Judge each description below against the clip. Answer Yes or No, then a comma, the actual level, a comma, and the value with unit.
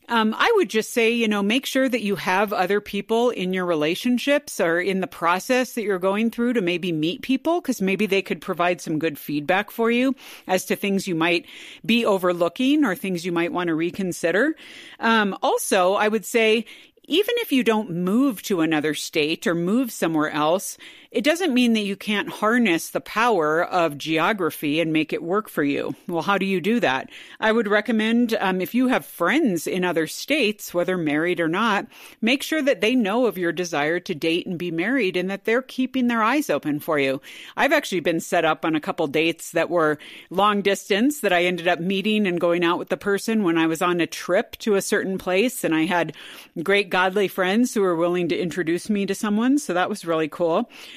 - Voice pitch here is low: No, high, 195 Hz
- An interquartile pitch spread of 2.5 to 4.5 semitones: No, average, 5.1 semitones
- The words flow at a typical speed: No, fast, 215 wpm